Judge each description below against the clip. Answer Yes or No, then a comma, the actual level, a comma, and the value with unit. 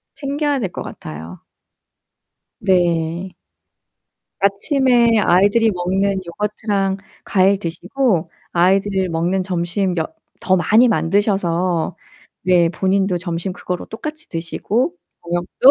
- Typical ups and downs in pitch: Yes, average, 3.1 semitones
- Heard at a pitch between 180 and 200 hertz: Yes, high, 190 Hz